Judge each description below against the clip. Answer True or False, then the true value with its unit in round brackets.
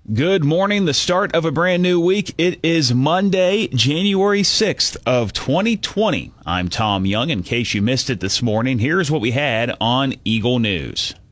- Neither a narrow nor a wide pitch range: False (7.9 semitones)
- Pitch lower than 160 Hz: True (135 Hz)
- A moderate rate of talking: True (175 wpm)